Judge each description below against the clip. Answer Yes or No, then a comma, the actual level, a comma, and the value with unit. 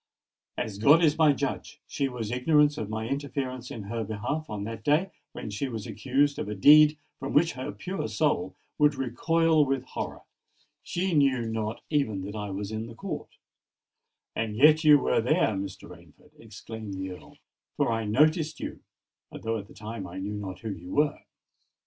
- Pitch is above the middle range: No, low, 115 Hz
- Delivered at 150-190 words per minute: Yes, average, 180 wpm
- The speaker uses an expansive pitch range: Yes, wide, 5.8 semitones